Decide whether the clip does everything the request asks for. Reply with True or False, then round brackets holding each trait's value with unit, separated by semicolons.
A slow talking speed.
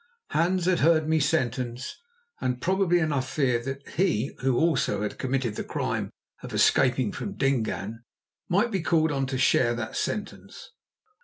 False (155 wpm)